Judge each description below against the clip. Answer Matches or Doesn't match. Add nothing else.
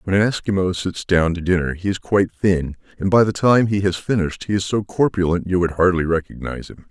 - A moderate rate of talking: Doesn't match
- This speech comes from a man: Matches